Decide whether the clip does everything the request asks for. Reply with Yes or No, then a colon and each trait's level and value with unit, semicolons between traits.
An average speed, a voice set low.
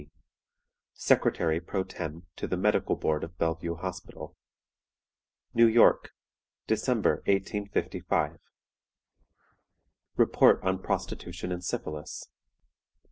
No: slow, 90 wpm; very low, 90 Hz